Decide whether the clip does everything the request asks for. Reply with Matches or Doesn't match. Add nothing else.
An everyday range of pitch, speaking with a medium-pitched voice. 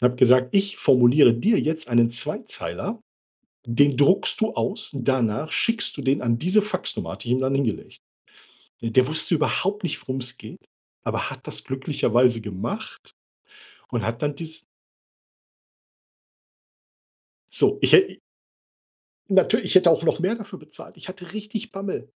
Doesn't match